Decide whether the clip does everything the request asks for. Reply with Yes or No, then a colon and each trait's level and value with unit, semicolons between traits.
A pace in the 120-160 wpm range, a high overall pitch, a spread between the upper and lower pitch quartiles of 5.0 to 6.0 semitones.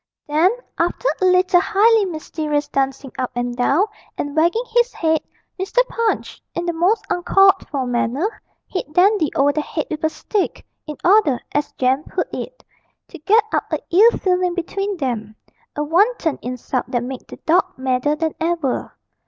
No: average, 170 wpm; very high, 325 Hz; wide, 5.5 semitones